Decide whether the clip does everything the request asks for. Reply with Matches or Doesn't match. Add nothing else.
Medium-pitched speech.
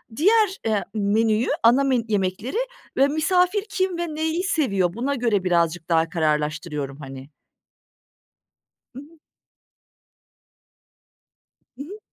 Doesn't match